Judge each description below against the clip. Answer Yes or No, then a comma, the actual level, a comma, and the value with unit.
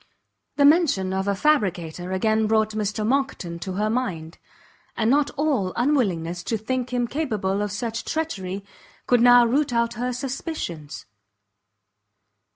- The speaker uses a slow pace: No, average, 145 wpm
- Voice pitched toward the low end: No, high, 220 Hz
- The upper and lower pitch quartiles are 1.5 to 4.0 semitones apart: No, average, 5.2 semitones